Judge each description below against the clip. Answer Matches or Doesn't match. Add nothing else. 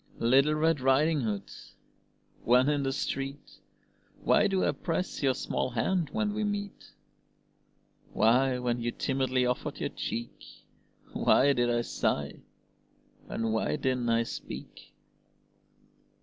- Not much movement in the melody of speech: Doesn't match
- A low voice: Matches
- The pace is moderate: Doesn't match